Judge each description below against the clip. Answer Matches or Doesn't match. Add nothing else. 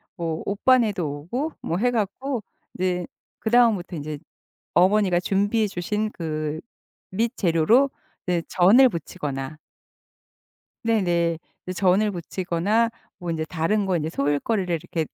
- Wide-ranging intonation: Doesn't match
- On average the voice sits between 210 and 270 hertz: Doesn't match